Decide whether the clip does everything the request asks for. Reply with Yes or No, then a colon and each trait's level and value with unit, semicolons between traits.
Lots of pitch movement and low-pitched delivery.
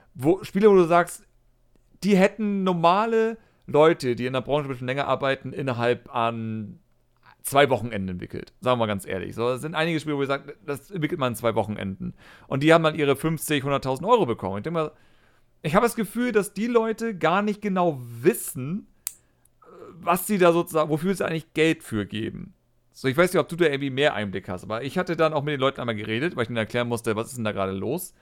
No: wide, 6.5 semitones; medium, 145 Hz